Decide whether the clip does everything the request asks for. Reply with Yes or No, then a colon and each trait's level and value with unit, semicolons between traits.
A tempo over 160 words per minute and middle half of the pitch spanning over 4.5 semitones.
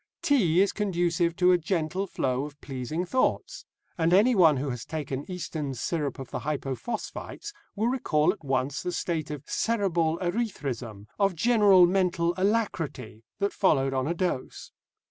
No: average, 150 wpm; wide, 5.4 semitones